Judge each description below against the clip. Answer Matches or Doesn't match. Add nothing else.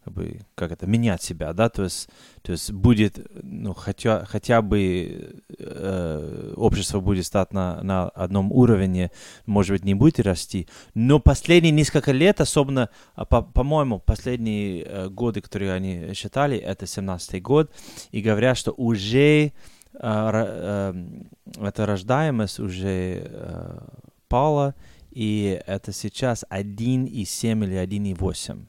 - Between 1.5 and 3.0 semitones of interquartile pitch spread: Doesn't match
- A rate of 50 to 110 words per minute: Doesn't match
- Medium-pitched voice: Doesn't match